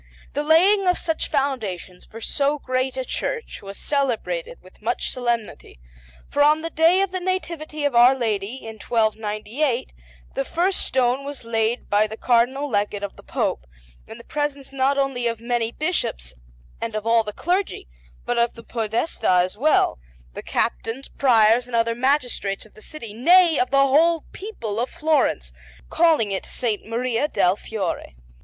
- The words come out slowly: No, average, 170 wpm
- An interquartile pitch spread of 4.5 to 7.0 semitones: Yes, average, 5.2 semitones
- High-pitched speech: Yes, very high, 250 Hz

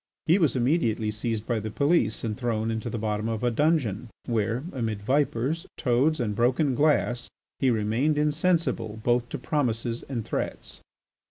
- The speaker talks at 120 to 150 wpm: No, average, 160 wpm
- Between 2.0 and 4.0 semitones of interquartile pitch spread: No, average, 4.6 semitones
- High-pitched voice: No, low, 120 Hz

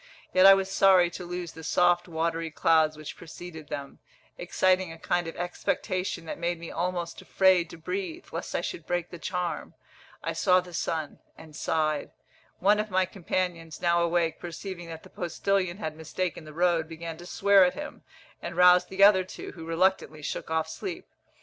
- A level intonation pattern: Yes, narrow, 2.2 semitones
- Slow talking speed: No, average, 185 wpm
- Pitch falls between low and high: Yes, medium, 175 Hz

